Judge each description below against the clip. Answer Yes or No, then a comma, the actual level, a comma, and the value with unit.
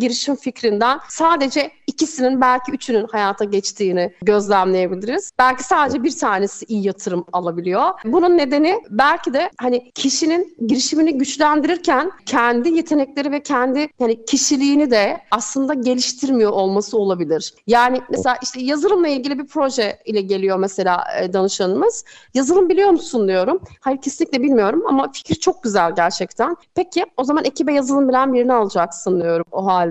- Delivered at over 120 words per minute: Yes, fast, 140 wpm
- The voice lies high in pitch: Yes, very high, 255 Hz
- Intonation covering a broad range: Yes, wide, 6.3 semitones